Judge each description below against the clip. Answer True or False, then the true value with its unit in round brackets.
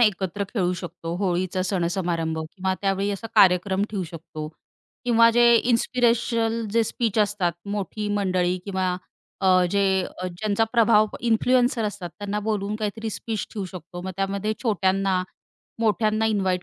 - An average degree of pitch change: True (3.3 semitones)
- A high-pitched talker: True (200 Hz)